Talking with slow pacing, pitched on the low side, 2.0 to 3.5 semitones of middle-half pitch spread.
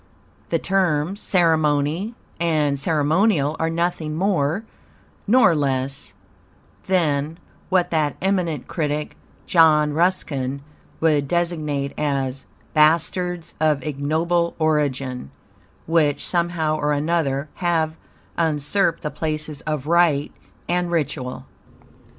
No: slow, 95 wpm; medium, 155 Hz; average, 2.9 semitones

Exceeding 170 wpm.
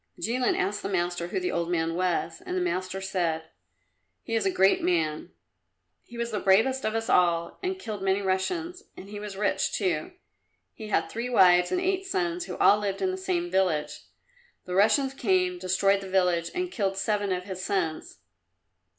Yes: average, 190 wpm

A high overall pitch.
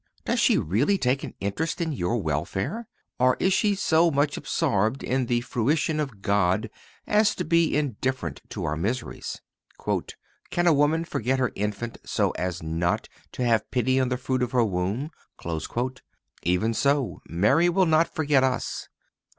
No: low, 125 Hz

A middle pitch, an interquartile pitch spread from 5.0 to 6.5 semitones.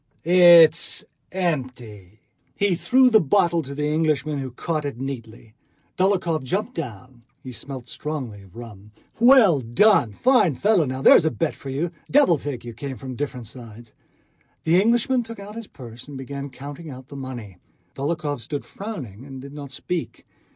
Yes: medium, 145 Hz; wide, 5.6 semitones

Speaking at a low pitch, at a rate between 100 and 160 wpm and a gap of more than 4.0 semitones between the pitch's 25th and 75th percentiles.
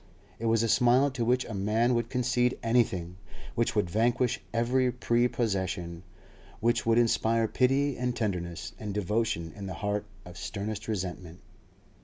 No: low, 115 Hz; average, 150 wpm; average, 3.6 semitones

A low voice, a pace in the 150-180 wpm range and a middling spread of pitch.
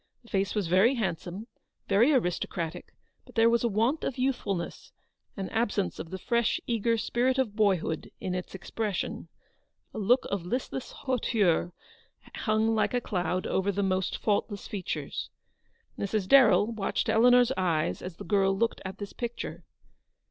No: high, 210 Hz; average, 155 wpm; average, 3.8 semitones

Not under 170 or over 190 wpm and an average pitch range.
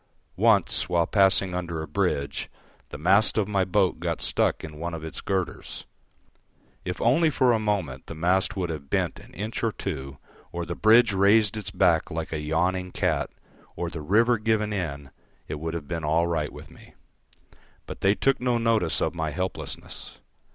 Yes: average, 185 wpm; average, 4.4 semitones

